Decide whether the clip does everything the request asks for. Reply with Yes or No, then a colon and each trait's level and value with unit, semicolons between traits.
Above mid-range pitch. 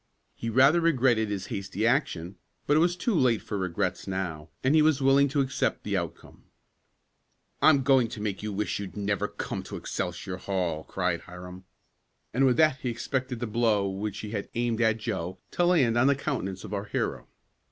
No: low, 115 Hz